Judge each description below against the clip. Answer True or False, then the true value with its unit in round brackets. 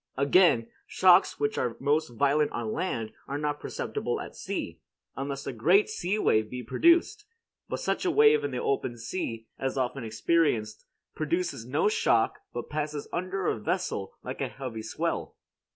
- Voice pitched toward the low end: False (145 Hz)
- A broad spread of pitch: True (7.6 semitones)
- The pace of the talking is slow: False (165 wpm)